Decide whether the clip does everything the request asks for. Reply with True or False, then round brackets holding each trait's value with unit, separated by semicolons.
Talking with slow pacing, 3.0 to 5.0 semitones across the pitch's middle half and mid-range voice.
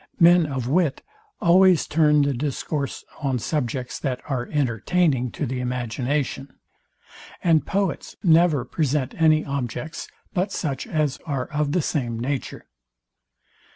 True (125 wpm; 3.9 semitones; 145 Hz)